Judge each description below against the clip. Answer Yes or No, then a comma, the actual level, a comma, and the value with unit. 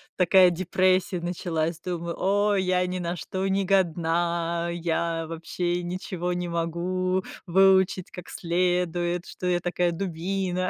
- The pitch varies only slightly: Yes, narrow, 1.4 semitones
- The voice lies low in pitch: No, medium, 180 Hz